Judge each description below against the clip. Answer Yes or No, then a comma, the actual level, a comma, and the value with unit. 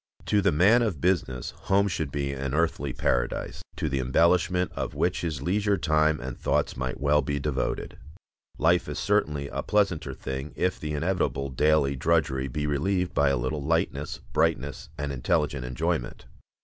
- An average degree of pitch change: Yes, average, 3.9 semitones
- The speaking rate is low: No, average, 165 wpm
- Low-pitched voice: Yes, very low, 75 Hz